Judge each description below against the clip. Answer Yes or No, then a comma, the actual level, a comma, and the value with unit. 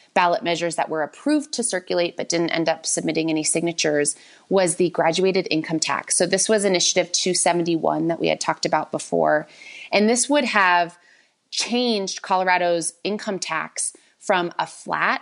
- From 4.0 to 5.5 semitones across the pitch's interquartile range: No, average, 2.9 semitones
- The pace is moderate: Yes, average, 160 wpm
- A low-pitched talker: No, medium, 175 Hz